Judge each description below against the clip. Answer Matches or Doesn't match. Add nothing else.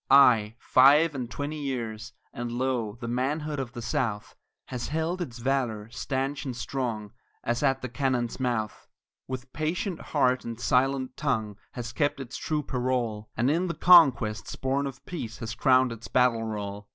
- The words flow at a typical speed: Matches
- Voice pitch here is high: Doesn't match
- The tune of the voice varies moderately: Matches